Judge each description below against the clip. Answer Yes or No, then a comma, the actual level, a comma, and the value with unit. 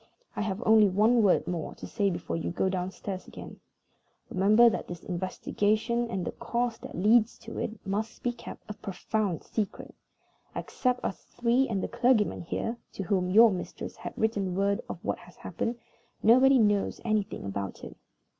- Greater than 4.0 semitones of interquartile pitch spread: No, average, 3.5 semitones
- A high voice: Yes, high, 210 Hz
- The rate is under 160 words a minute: No, average, 175 wpm